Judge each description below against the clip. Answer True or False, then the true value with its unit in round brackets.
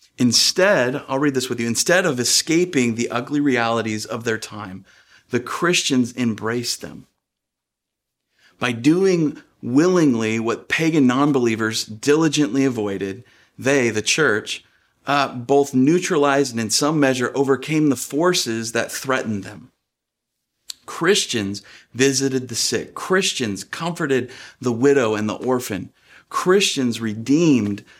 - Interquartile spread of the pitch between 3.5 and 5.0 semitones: True (4.2 semitones)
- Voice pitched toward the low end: True (125 Hz)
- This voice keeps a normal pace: False (120 wpm)